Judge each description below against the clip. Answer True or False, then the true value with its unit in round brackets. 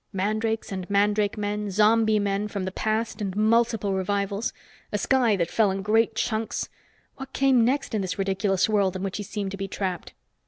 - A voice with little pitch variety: True (2.1 semitones)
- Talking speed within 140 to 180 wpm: False (190 wpm)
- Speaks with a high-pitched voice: True (205 Hz)